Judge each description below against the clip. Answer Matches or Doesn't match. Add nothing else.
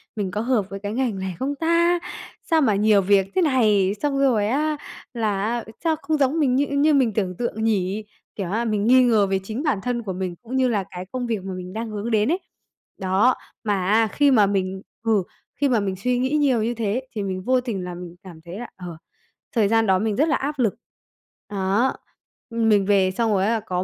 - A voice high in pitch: Matches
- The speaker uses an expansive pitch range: Doesn't match